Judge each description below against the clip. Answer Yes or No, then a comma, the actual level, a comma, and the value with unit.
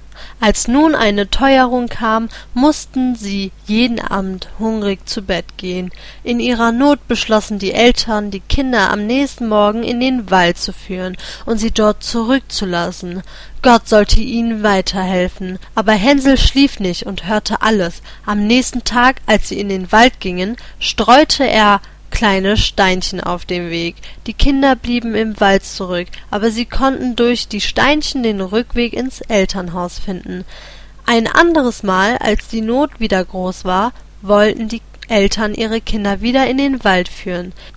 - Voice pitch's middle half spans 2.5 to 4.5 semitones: Yes, average, 4.0 semitones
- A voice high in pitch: Yes, high, 220 Hz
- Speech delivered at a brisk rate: Yes, fast, 155 wpm